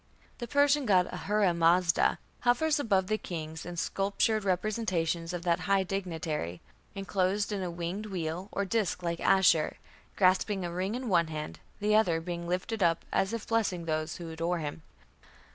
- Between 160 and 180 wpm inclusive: Yes, average, 170 wpm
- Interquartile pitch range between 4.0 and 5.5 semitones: No, average, 3.5 semitones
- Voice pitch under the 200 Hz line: Yes, medium, 185 Hz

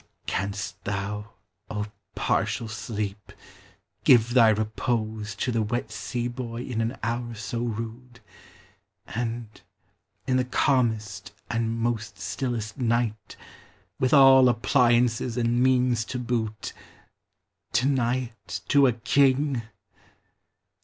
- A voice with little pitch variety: Yes, narrow, 2.3 semitones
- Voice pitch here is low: Yes, low, 115 Hz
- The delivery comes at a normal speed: No, slow, 110 wpm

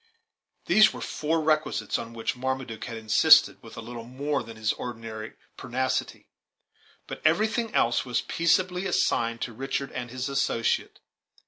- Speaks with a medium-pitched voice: No, low, 125 Hz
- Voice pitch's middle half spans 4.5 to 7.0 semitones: Yes, average, 5.0 semitones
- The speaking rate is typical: Yes, average, 145 wpm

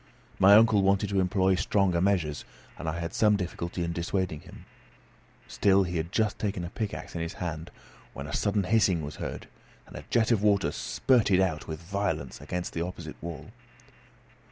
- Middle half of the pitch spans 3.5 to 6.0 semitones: No, average, 3.1 semitones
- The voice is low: Yes, very low, 95 Hz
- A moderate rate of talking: Yes, average, 180 wpm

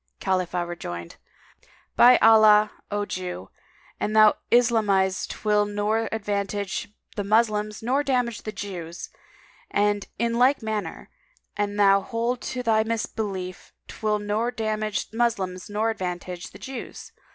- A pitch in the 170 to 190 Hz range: No, high, 210 Hz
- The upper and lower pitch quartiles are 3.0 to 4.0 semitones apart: No, narrow, 2.4 semitones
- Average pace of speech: No, slow, 130 wpm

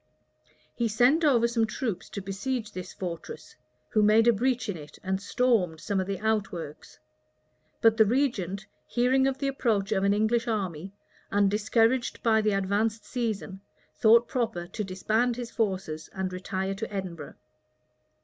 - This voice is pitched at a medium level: No, high, 215 Hz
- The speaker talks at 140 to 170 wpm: Yes, average, 160 wpm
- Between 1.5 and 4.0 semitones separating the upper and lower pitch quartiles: Yes, average, 3.5 semitones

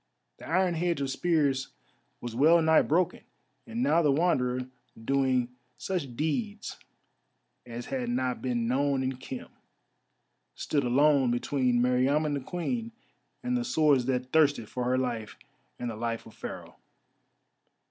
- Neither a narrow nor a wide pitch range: Yes, average, 4.3 semitones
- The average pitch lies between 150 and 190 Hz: No, low, 135 Hz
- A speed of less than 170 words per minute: Yes, average, 140 wpm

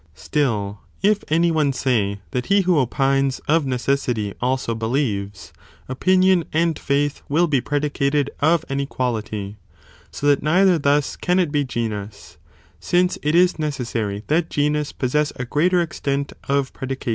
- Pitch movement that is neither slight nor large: Yes, average, 4.2 semitones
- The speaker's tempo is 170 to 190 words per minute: No, average, 145 wpm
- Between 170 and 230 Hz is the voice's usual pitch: No, medium, 140 Hz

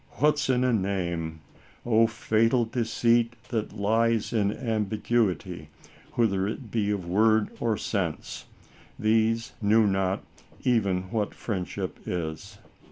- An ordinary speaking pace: No, slow, 125 wpm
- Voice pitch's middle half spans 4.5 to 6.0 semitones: No, average, 2.8 semitones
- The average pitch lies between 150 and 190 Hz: No, low, 110 Hz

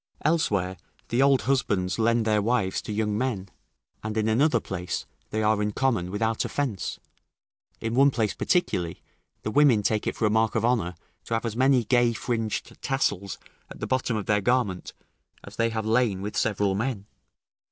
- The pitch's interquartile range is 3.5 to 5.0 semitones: No, average, 3.1 semitones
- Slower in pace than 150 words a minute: No, average, 180 wpm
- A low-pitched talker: Yes, low, 110 Hz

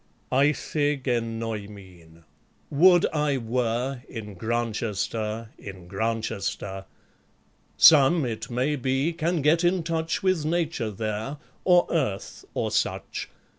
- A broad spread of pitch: Yes, wide, 5.8 semitones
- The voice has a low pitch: Yes, low, 125 Hz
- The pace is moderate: No, slow, 110 wpm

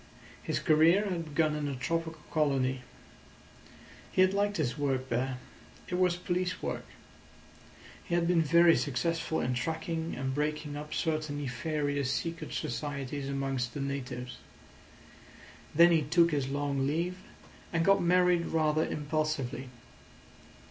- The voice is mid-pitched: Yes, medium, 150 Hz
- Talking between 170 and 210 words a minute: No, slow, 135 wpm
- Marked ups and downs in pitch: No, average, 3.4 semitones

